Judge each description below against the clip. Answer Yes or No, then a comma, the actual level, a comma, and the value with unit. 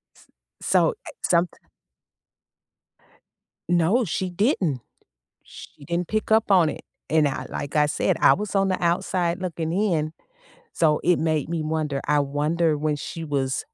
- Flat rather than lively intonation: No, average, 3.1 semitones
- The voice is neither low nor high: Yes, medium, 165 Hz